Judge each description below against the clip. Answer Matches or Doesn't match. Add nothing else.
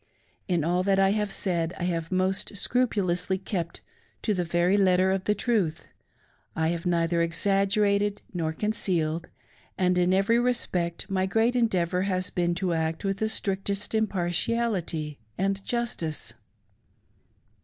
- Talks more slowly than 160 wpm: Matches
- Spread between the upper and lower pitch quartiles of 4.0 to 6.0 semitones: Doesn't match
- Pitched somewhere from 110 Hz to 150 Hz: Doesn't match